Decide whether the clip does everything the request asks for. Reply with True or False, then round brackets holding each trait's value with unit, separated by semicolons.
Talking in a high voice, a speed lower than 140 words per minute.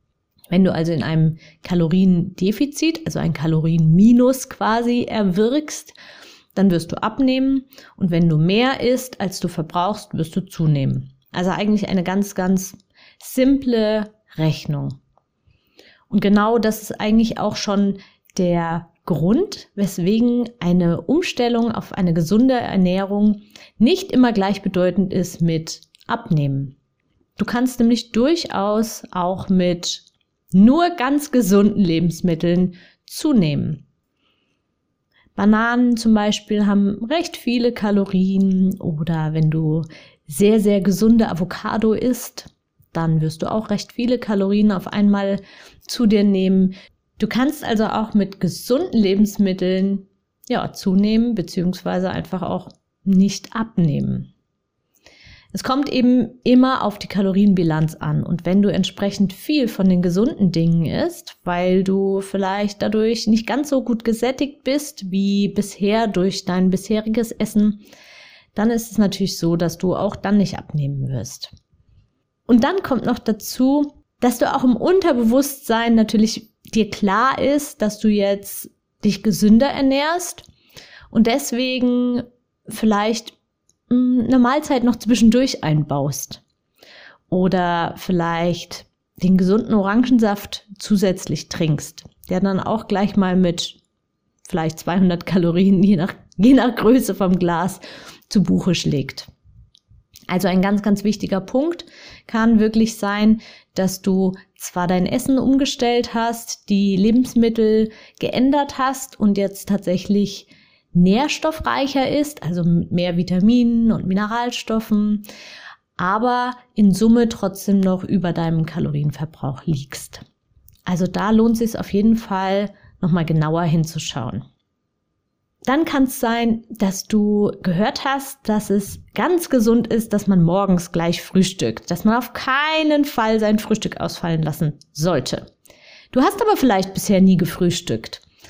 True (200 Hz; 125 wpm)